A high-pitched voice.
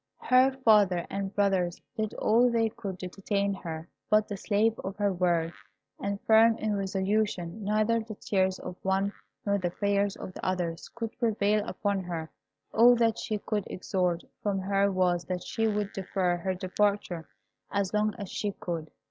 Yes: high, 200 Hz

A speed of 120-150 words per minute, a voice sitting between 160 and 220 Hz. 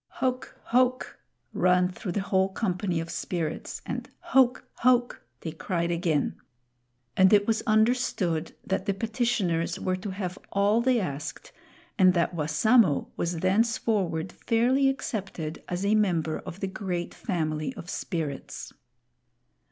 Yes: slow, 135 wpm; high, 190 Hz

